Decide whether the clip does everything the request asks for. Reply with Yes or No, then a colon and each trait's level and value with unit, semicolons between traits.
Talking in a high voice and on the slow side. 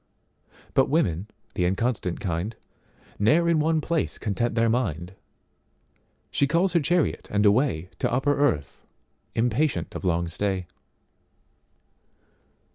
No: low, 115 Hz; slow, 100 wpm